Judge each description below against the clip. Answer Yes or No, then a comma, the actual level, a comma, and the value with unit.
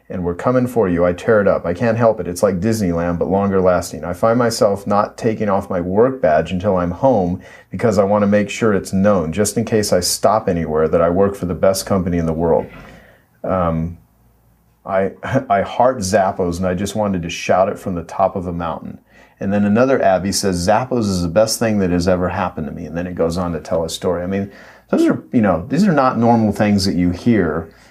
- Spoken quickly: Yes, fast, 240 wpm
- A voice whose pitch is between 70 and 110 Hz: Yes, very low, 95 Hz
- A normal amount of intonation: Yes, average, 3.1 semitones